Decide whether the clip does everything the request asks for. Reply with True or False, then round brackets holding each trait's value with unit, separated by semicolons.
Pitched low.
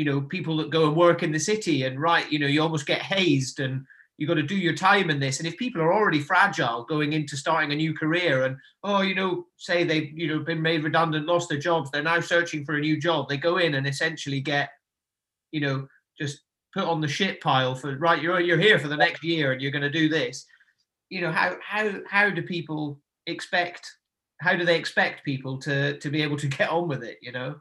False (160 Hz)